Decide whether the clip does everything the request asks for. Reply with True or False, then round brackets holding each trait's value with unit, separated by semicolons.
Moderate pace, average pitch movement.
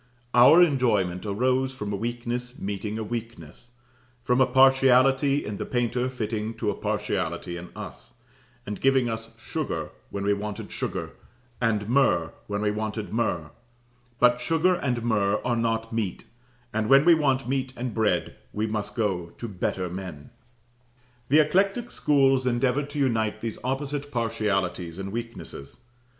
True (150 wpm; 4.1 semitones)